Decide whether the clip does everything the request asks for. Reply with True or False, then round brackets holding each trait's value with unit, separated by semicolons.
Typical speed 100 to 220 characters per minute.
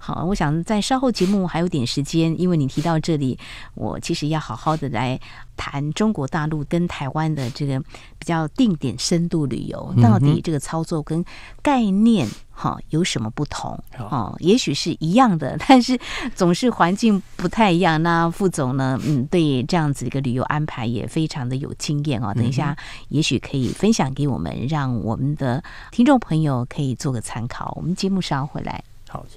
False (280 characters per minute)